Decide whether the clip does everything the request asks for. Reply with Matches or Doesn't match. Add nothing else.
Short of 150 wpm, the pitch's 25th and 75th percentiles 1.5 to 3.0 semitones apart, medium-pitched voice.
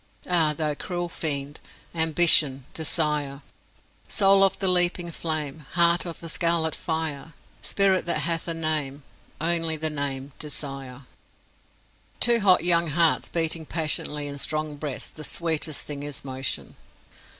Matches